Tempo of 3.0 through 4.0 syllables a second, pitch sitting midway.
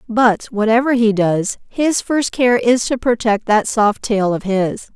No: 3.9 syllables/s; high, 225 Hz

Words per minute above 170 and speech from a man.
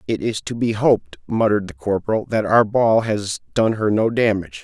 Yes: fast, 205 wpm; male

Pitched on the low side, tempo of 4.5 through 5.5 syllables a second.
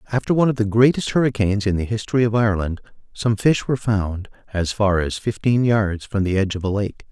No: low, 105 Hz; 6.2 syllables/s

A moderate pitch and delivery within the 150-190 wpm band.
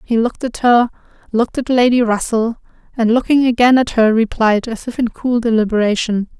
No: high, 235 Hz; average, 180 wpm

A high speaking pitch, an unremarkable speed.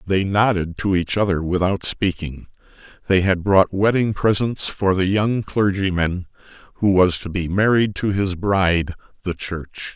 No: very low, 95 Hz; average, 150 wpm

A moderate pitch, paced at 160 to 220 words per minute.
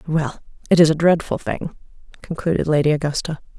No: medium, 160 Hz; average, 150 wpm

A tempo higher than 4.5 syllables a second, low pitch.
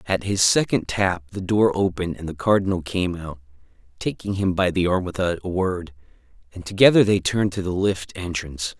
Yes: 5.4 syllables/s; very low, 90 Hz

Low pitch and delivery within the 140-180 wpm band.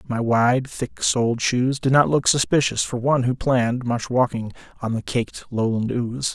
No: low, 125 Hz; average, 190 wpm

